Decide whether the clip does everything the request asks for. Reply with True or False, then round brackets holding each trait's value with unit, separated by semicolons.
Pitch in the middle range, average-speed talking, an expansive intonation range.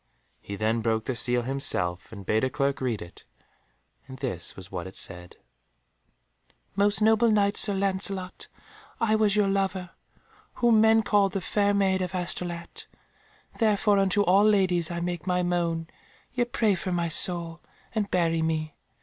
True (180 Hz; 160 wpm; 6.6 semitones)